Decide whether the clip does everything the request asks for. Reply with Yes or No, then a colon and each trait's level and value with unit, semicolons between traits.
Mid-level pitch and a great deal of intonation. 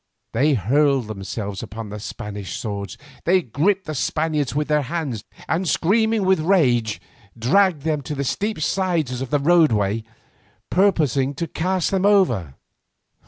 Yes: medium, 145 Hz; wide, 7.6 semitones